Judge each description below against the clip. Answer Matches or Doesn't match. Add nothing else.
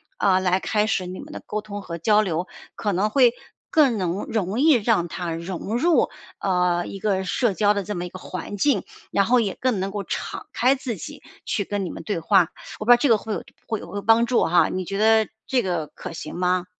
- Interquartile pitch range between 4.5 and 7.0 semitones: Doesn't match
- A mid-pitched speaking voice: Doesn't match